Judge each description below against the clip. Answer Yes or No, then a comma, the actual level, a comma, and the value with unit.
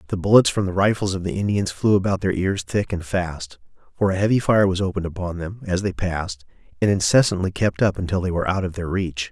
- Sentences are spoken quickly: Yes, fast, 240 wpm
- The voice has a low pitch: Yes, very low, 95 Hz